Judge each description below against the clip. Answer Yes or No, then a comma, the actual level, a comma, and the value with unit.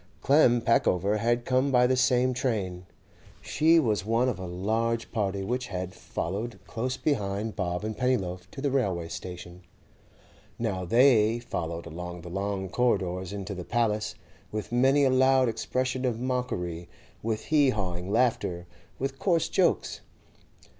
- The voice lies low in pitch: Yes, low, 110 Hz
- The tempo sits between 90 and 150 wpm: Yes, average, 145 wpm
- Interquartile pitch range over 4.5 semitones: Yes, wide, 5.5 semitones